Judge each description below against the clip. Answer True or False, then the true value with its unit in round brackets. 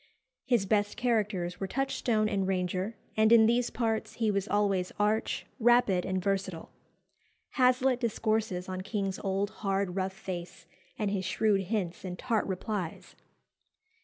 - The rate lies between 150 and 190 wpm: False (140 wpm)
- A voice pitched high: True (205 Hz)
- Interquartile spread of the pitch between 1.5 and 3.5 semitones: True (2.9 semitones)